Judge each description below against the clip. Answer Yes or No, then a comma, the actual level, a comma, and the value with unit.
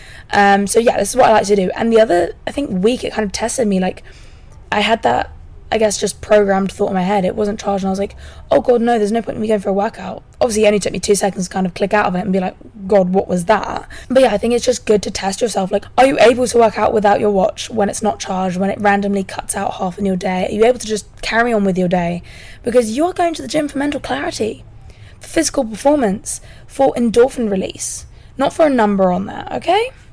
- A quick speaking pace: Yes, fast, 275 wpm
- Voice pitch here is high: Yes, high, 210 Hz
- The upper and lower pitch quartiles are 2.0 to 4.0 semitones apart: Yes, average, 3.3 semitones